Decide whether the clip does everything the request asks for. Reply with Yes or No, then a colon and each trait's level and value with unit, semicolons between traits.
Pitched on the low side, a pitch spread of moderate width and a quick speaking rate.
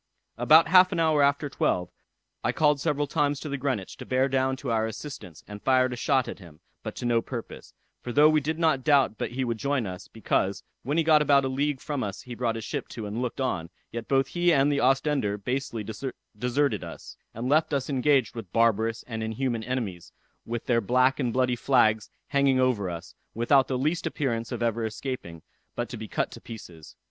Yes: low, 130 Hz; average, 3.9 semitones; fast, 215 wpm